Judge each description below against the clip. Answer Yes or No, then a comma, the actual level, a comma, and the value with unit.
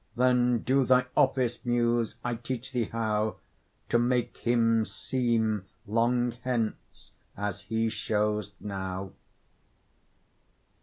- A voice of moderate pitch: No, low, 115 Hz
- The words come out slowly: Yes, slow, 105 wpm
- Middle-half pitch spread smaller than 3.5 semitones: Yes, narrow, 2.4 semitones